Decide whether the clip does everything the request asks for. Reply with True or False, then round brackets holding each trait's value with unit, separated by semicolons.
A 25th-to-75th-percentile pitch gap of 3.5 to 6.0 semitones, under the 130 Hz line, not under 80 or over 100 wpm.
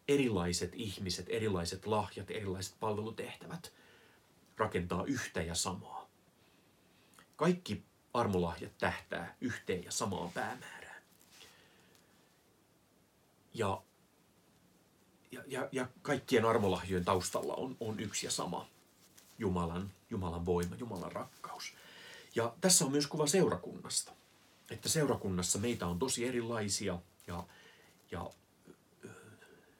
True (4.5 semitones; 95 Hz; 95 wpm)